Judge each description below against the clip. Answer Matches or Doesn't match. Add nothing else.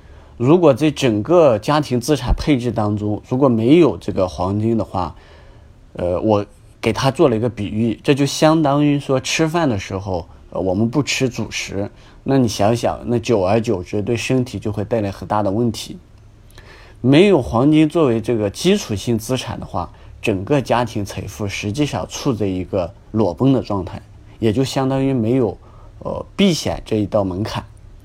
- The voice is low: Matches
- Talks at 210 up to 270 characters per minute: Matches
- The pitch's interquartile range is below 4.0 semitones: Doesn't match